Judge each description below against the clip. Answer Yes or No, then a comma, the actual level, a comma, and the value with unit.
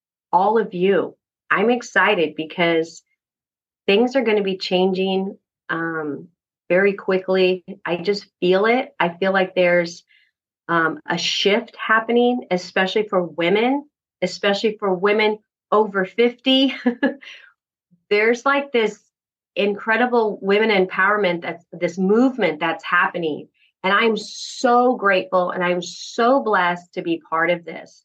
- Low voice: No, high, 195 Hz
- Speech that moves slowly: Yes, slow, 125 wpm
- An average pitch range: Yes, average, 3.9 semitones